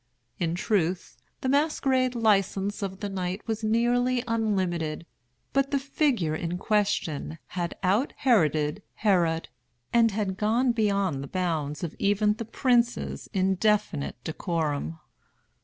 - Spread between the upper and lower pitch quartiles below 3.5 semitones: No, average, 5.1 semitones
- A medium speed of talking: No, slow, 120 wpm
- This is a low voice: No, high, 200 Hz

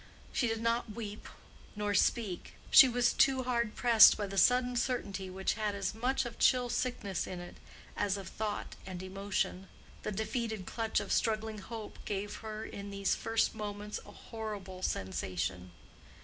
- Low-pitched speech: No, high, 215 Hz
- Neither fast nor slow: Yes, average, 165 wpm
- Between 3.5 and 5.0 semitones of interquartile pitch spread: No, average, 2.9 semitones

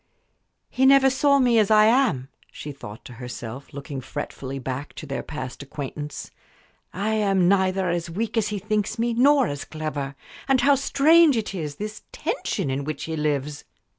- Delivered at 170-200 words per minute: Yes, average, 175 wpm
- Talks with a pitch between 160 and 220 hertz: Yes, medium, 185 Hz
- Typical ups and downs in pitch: No, wide, 8.3 semitones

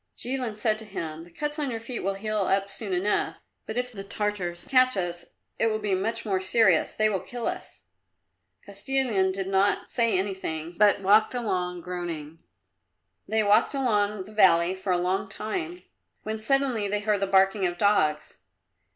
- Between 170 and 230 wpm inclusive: Yes, average, 175 wpm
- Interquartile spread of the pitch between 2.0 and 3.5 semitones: Yes, average, 2.9 semitones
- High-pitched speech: Yes, high, 205 Hz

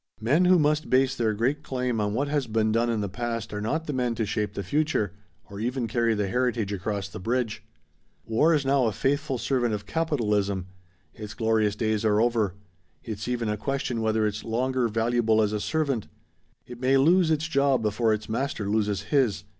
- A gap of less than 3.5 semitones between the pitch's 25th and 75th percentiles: No, average, 4.0 semitones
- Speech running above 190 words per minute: Yes, average, 200 wpm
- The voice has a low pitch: Yes, low, 115 Hz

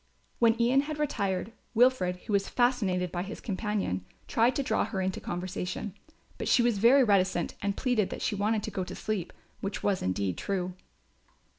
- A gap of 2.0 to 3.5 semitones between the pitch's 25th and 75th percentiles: No, average, 4.3 semitones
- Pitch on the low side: No, high, 200 Hz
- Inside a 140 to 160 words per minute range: No, average, 180 wpm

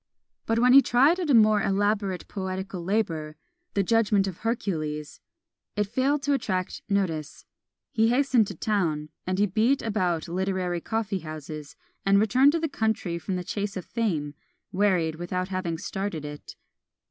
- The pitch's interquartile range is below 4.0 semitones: No, average, 4.3 semitones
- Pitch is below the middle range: No, high, 195 Hz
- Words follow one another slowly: No, average, 160 wpm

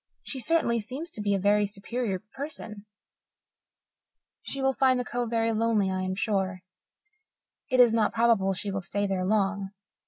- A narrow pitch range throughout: No, average, 3.8 semitones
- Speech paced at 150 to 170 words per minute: Yes, average, 165 wpm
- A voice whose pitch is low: No, high, 215 Hz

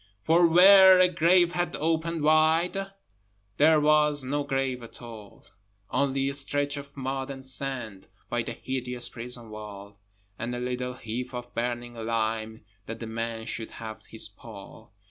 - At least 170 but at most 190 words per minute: No, average, 155 wpm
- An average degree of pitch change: Yes, average, 4.8 semitones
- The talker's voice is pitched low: Yes, low, 130 Hz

